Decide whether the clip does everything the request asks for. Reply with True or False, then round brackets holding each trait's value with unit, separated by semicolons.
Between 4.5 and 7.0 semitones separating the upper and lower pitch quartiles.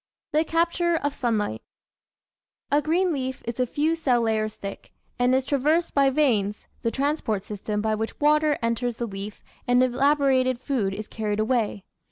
True (5.2 semitones)